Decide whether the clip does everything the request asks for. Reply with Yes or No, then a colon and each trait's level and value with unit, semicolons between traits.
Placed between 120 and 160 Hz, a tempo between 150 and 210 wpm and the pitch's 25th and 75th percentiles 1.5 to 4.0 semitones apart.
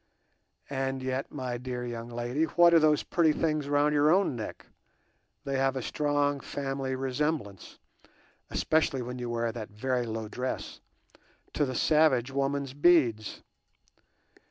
No: low, 135 Hz; slow, 135 wpm; average, 3.3 semitones